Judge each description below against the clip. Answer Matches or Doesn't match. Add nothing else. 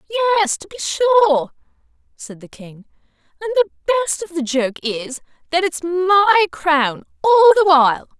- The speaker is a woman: Matches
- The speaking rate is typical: Matches